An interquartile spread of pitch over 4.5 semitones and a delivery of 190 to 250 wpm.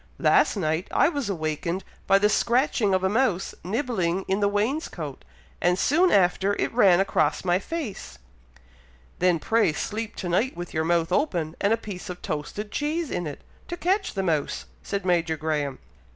No: average, 5.1 semitones; average, 175 wpm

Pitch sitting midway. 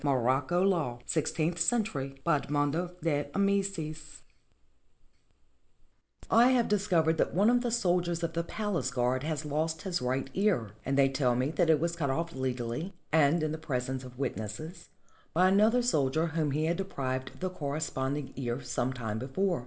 Yes: medium, 155 Hz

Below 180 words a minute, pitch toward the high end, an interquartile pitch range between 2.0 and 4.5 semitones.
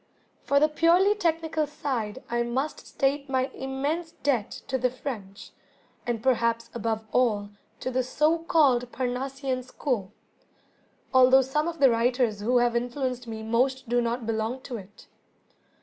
Yes: average, 150 wpm; very high, 255 Hz; average, 3.1 semitones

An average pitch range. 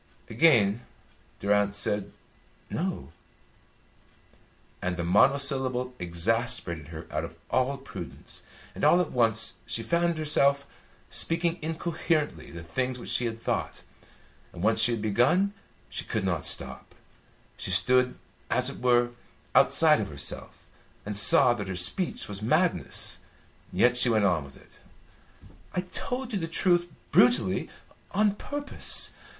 No: wide, 7.6 semitones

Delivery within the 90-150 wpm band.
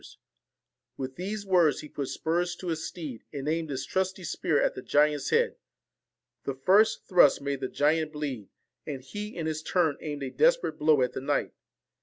No: average, 190 wpm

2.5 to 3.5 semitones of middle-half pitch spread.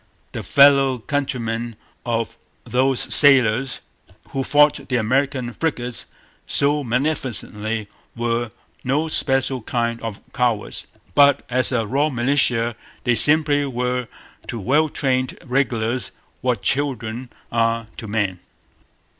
Yes: average, 3.0 semitones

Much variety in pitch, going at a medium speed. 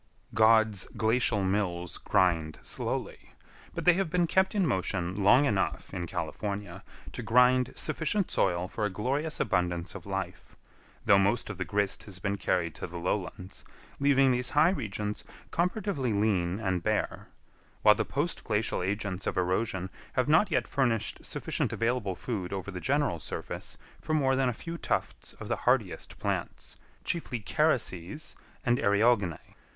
Yes: wide, 6.0 semitones; average, 155 wpm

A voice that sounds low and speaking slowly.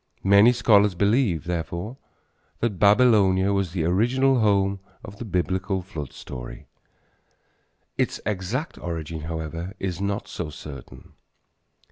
Yes: very low, 95 Hz; slow, 115 wpm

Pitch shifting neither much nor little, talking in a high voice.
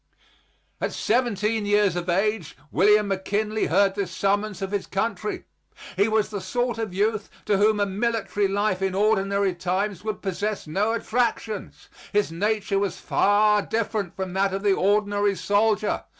No: narrow, 1.7 semitones; high, 205 Hz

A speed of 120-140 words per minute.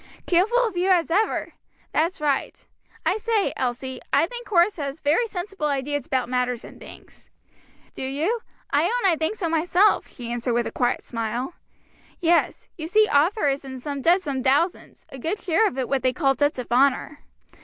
No: average, 185 wpm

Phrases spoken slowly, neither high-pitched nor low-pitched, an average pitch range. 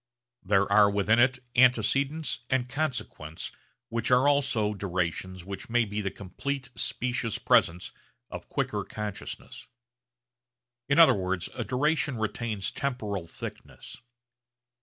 No: slow, 115 wpm; low, 110 Hz; average, 4.4 semitones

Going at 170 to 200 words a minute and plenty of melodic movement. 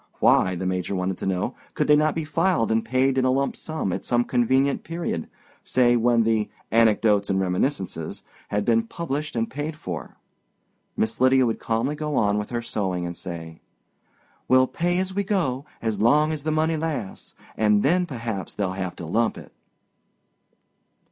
Yes: average, 175 wpm; wide, 6.5 semitones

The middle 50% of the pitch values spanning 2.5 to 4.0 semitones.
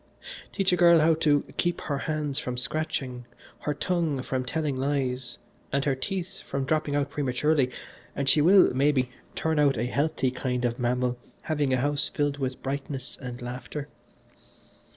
Yes: average, 3.1 semitones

